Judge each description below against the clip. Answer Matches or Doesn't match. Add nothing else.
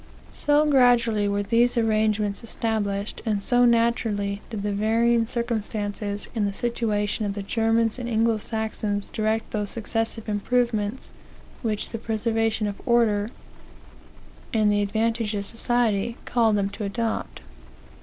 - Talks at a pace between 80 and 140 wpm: Matches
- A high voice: Matches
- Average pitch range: Doesn't match